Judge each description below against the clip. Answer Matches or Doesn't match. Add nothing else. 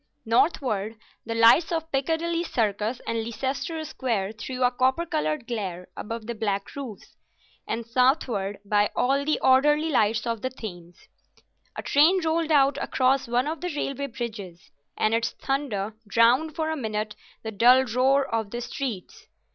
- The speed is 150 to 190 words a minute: Matches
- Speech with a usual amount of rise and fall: Matches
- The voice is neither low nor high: Doesn't match